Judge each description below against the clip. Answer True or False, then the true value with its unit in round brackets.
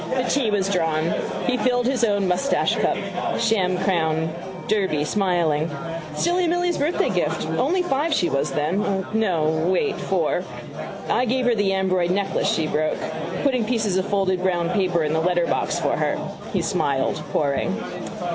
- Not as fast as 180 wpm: True (155 wpm)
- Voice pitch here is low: False (190 Hz)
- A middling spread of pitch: False (6.0 semitones)